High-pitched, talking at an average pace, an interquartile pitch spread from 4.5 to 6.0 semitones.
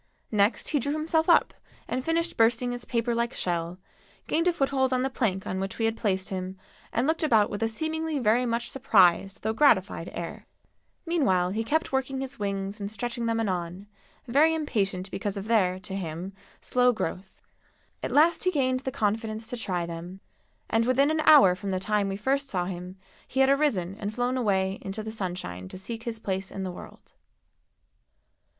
Yes: high, 220 Hz; average, 190 wpm; wide, 5.5 semitones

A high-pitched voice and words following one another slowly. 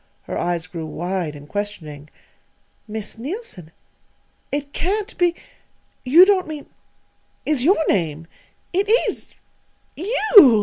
Yes: high, 240 Hz; slow, 115 wpm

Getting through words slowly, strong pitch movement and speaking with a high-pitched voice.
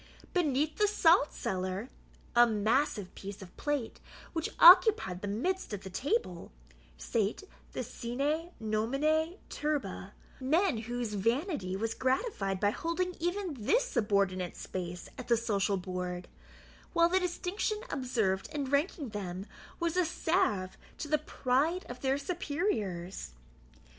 Yes: slow, 130 wpm; wide, 8.9 semitones; very high, 255 Hz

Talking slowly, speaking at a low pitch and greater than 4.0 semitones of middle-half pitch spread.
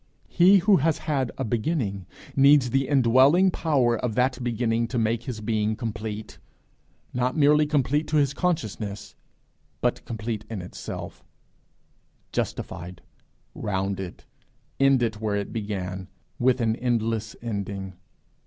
Yes: slow, 125 wpm; low, 115 Hz; average, 4.4 semitones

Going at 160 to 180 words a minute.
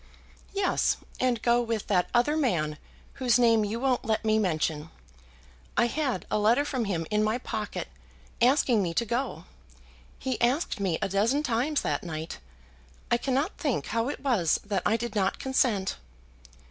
Yes: average, 165 wpm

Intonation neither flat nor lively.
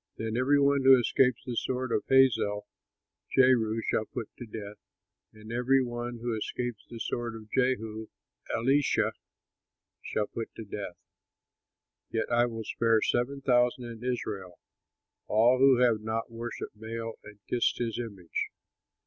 No: narrow, 2.3 semitones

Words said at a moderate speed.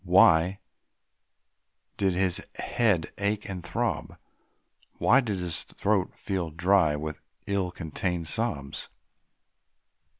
No: slow, 100 wpm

